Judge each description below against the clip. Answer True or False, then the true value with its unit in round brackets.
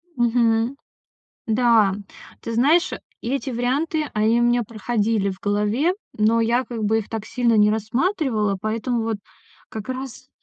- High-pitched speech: True (230 Hz)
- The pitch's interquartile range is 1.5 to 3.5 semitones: True (2.6 semitones)